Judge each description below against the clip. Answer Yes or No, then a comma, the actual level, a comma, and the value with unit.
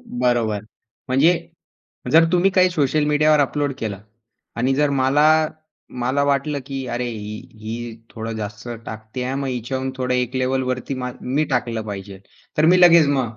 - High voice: No, low, 130 Hz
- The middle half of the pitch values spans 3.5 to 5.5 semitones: Yes, average, 3.8 semitones